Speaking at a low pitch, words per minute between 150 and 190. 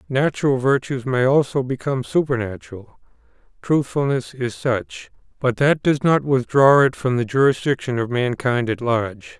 No: low, 130 Hz; average, 140 wpm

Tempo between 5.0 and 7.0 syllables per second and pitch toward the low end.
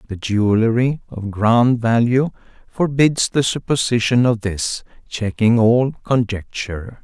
No: 4.1 syllables/s; low, 115 Hz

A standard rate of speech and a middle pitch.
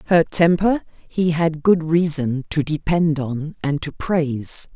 Yes: average, 150 wpm; medium, 160 Hz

